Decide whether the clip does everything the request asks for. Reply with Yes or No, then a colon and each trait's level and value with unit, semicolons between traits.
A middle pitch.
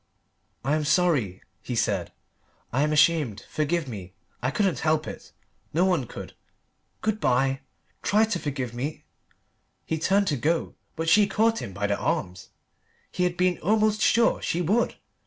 Yes: medium, 155 Hz